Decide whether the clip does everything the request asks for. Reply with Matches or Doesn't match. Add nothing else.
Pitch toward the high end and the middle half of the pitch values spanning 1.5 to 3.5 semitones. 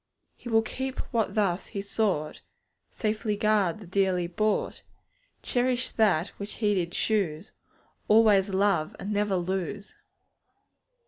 Matches